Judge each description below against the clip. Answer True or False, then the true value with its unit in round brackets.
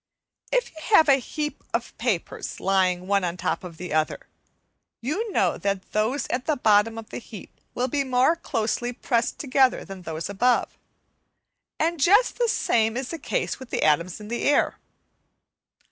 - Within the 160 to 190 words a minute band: True (175 wpm)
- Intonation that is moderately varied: False (6.0 semitones)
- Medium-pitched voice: False (235 Hz)